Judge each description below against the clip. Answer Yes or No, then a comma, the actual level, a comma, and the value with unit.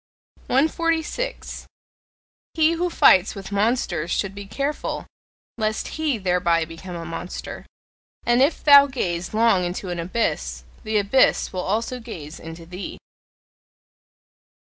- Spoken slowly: Yes, slow, 120 wpm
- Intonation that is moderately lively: No, wide, 7.0 semitones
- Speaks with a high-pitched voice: Yes, high, 200 Hz